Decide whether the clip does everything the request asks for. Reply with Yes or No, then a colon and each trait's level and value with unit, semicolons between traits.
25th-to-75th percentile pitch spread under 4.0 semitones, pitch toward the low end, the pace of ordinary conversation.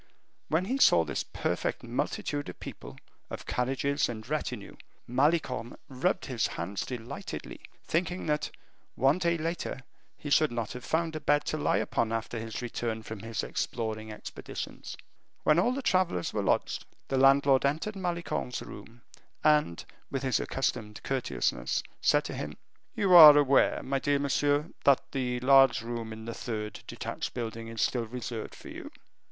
No: average, 4.7 semitones; low, 130 Hz; average, 160 wpm